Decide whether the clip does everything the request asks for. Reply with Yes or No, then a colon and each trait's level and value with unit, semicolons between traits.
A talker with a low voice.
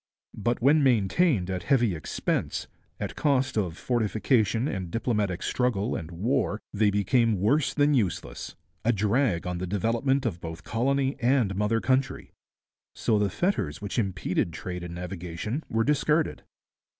Yes: low, 110 Hz